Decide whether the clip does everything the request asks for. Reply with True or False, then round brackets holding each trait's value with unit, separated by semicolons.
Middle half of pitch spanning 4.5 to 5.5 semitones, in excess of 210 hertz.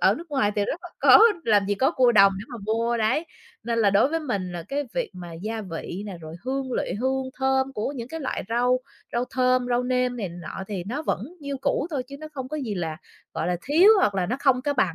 True (4.9 semitones; 245 Hz)